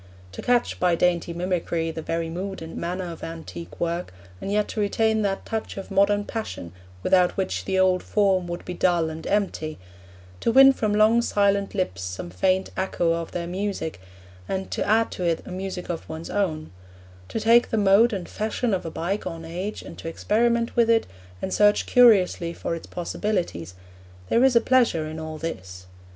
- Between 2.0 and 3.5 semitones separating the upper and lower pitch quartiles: No, average, 4.0 semitones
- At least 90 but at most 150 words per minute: No, average, 190 wpm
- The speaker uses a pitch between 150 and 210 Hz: Yes, medium, 185 Hz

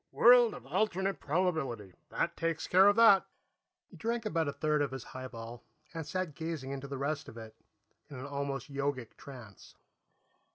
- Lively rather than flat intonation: Yes, wide, 5.7 semitones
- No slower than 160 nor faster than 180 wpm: Yes, average, 170 wpm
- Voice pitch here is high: No, medium, 145 Hz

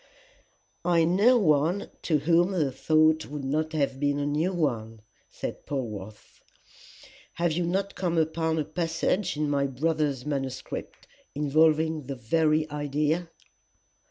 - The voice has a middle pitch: Yes, medium, 155 Hz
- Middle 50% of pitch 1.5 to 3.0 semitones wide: Yes, narrow, 2.6 semitones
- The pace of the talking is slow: Yes, slow, 130 wpm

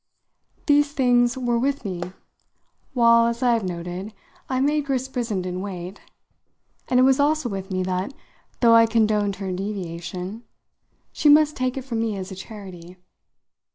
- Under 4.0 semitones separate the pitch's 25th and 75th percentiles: No, average, 5.3 semitones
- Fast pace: No, average, 155 wpm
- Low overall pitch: No, high, 225 Hz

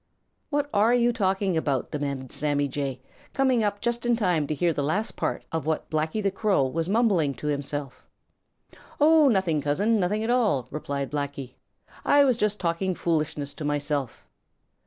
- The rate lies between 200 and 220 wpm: No, average, 170 wpm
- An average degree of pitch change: No, wide, 6.9 semitones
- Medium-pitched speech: Yes, medium, 165 Hz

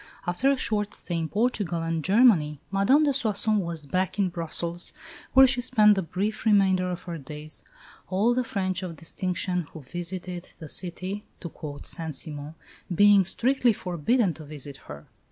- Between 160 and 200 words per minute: Yes, average, 170 wpm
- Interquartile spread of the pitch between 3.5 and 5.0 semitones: Yes, average, 4.3 semitones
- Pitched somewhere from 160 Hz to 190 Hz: Yes, medium, 185 Hz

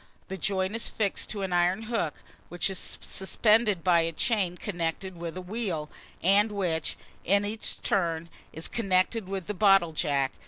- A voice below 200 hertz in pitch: Yes, high, 190 Hz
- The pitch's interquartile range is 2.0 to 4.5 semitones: Yes, average, 3.3 semitones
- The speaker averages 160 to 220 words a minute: Yes, average, 165 wpm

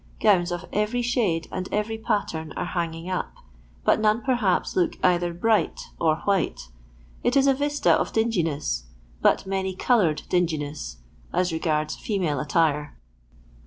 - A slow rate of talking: No, average, 145 wpm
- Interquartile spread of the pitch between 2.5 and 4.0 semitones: No, average, 5.0 semitones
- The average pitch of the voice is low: No, medium, 180 Hz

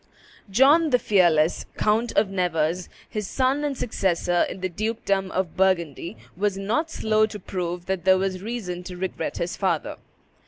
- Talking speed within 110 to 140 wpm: No, average, 160 wpm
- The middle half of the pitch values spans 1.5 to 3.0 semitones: No, average, 3.5 semitones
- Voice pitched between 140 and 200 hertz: Yes, high, 190 Hz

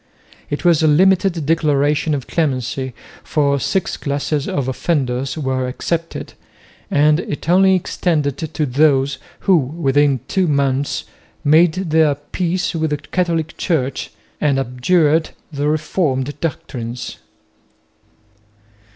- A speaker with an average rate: No, slow, 115 wpm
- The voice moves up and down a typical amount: Yes, average, 3.3 semitones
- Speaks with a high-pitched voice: No, medium, 150 Hz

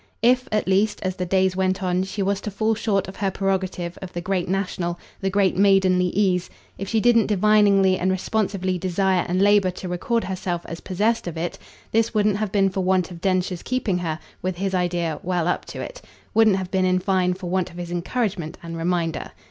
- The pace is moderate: No, fast, 210 wpm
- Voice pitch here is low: No, high, 190 Hz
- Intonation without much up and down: Yes, narrow, 2.0 semitones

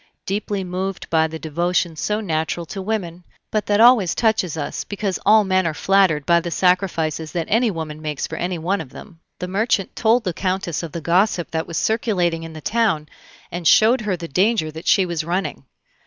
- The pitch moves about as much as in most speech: Yes, average, 3.8 semitones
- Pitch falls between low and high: Yes, medium, 180 Hz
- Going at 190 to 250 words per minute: Yes, average, 200 wpm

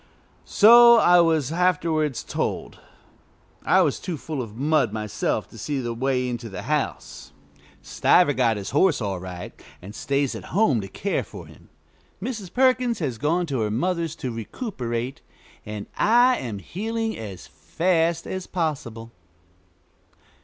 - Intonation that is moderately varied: No, wide, 7.7 semitones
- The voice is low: No, medium, 145 Hz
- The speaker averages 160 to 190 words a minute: No, average, 145 wpm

